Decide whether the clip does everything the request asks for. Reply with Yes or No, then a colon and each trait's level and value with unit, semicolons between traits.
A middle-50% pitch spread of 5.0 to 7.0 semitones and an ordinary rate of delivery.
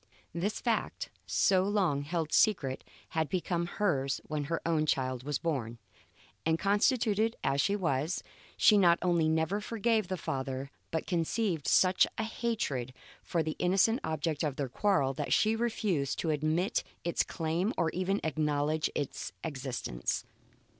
Yes: wide, 5.4 semitones; average, 150 wpm